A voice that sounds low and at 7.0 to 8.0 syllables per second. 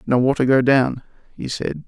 No: low, 130 Hz; 4.8 syllables/s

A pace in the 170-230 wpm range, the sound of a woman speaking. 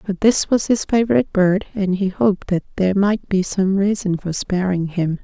Yes: fast, 205 wpm; female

